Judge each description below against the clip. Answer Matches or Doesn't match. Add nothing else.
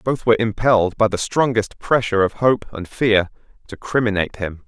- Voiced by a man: Matches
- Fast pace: Doesn't match